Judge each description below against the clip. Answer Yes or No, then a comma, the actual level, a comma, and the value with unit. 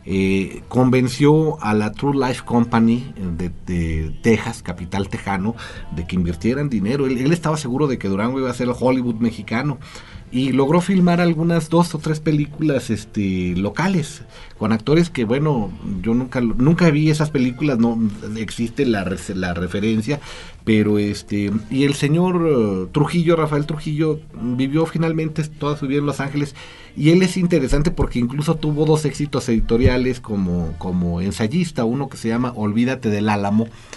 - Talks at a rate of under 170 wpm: Yes, average, 160 wpm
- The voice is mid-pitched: No, low, 125 Hz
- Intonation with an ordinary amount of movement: No, wide, 6.1 semitones